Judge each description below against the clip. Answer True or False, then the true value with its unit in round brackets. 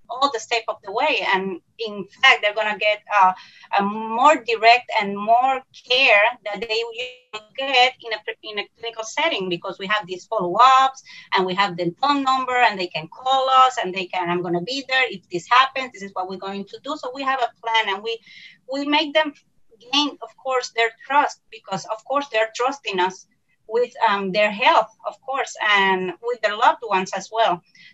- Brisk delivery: True (210 wpm)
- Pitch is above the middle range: True (230 Hz)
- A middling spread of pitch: True (5.0 semitones)